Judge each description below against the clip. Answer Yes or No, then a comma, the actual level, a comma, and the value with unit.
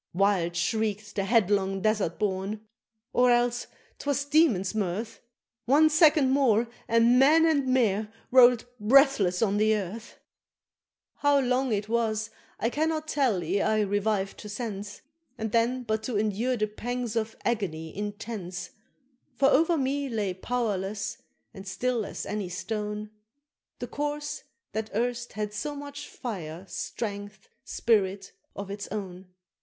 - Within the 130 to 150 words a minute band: Yes, average, 140 wpm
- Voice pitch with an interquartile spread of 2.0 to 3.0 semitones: No, average, 3.7 semitones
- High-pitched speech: Yes, high, 220 Hz